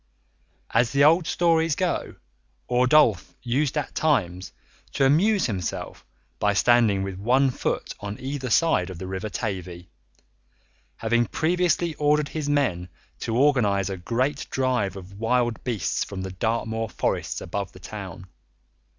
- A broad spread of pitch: Yes, wide, 6.8 semitones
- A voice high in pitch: No, low, 120 Hz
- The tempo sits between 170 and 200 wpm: No, average, 140 wpm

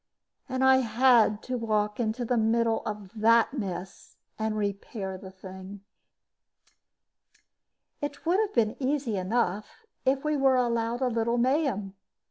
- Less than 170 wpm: Yes, slow, 135 wpm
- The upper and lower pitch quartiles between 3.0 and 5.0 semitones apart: Yes, average, 3.8 semitones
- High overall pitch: Yes, high, 230 Hz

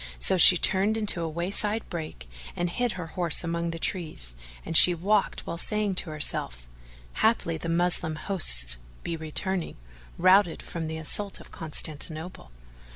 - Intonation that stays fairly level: No, average, 3.1 semitones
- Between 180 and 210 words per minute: No, average, 155 wpm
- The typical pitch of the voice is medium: Yes, medium, 170 Hz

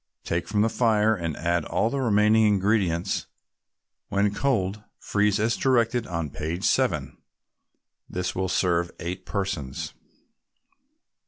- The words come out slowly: Yes, slow, 120 wpm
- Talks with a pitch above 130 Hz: No, low, 100 Hz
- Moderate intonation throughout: Yes, average, 4.0 semitones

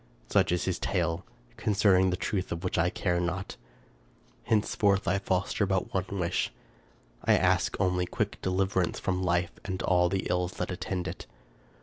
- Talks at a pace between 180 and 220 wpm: No, average, 165 wpm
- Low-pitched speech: Yes, very low, 95 Hz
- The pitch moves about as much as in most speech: No, narrow, 1.5 semitones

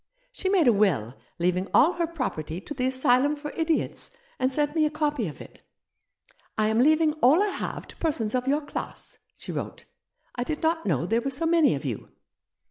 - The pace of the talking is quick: Yes, fast, 215 wpm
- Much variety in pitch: Yes, wide, 6.0 semitones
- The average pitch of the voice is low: No, very high, 275 Hz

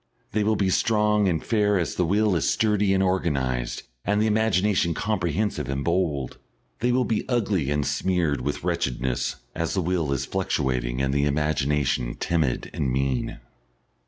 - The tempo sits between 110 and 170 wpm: Yes, average, 160 wpm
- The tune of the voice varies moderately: No, wide, 6.9 semitones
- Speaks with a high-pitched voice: No, very low, 85 Hz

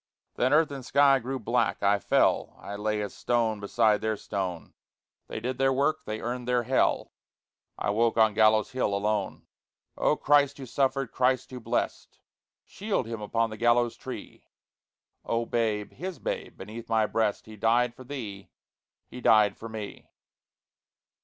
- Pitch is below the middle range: Yes, low, 115 Hz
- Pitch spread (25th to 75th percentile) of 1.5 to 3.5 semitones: Yes, average, 3.2 semitones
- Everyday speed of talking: Yes, average, 160 wpm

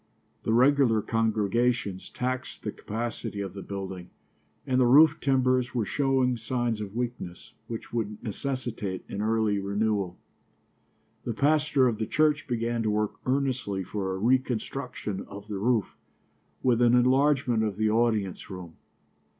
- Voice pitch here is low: Yes, low, 115 Hz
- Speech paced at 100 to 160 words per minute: Yes, average, 140 wpm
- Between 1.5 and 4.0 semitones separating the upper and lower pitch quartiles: Yes, average, 3.7 semitones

